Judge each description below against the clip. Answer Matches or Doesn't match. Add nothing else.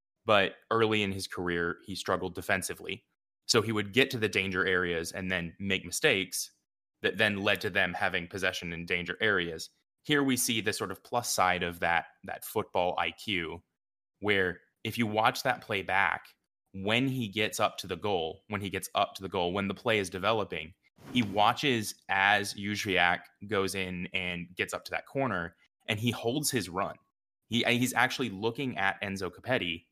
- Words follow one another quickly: Doesn't match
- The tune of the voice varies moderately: Matches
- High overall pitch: Doesn't match